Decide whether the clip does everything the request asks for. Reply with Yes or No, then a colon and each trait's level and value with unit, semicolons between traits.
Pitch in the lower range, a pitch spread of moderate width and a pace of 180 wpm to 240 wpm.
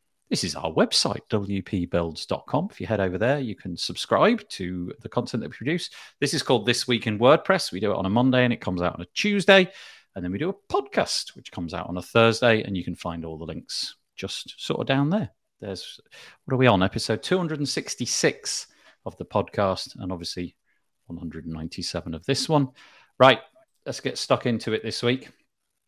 No: low, 110 Hz; wide, 6.7 semitones; average, 200 wpm